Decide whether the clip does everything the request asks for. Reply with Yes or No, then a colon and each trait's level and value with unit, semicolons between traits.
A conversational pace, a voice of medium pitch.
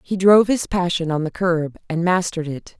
No: fast, 215 wpm; medium, 175 Hz